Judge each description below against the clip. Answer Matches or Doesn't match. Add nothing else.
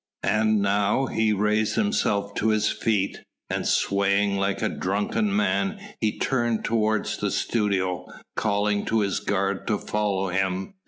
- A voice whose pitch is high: Doesn't match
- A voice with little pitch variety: Matches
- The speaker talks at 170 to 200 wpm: Doesn't match